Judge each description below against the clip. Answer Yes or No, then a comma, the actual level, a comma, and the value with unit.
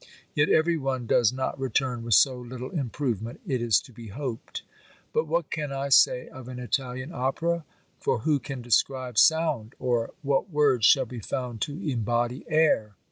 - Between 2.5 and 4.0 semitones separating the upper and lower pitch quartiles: Yes, average, 3.3 semitones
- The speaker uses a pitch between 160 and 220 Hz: No, low, 130 Hz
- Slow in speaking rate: No, average, 175 wpm